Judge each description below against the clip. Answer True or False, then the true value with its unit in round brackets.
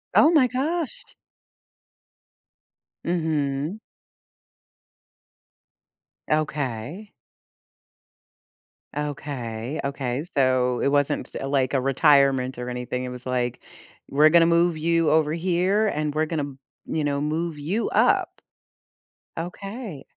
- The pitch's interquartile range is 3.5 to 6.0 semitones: True (4.1 semitones)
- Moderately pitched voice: True (150 Hz)